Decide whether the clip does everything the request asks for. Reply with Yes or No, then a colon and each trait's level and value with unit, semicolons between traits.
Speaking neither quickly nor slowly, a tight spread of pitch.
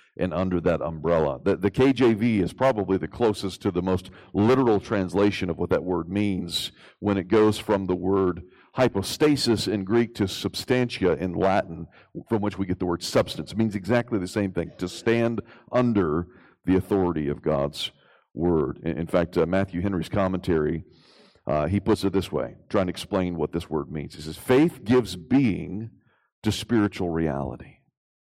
No: average, 175 wpm; average, 3.6 semitones